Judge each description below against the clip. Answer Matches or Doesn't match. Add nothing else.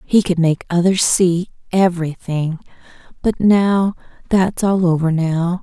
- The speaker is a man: Doesn't match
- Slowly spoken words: Matches